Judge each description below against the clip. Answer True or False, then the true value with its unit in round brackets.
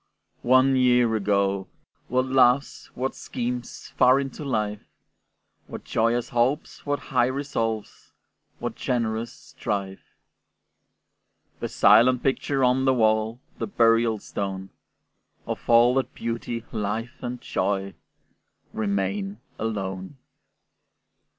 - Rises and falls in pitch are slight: False (3.4 semitones)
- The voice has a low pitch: True (115 Hz)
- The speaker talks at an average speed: False (105 wpm)